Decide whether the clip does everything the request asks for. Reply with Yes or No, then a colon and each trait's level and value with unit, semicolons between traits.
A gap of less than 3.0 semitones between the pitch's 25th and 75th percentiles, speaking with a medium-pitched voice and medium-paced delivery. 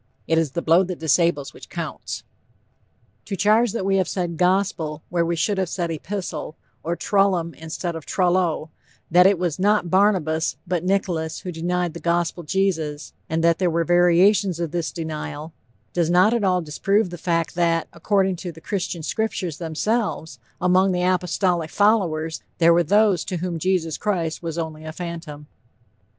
Yes: narrow, 2.5 semitones; medium, 175 Hz; average, 170 wpm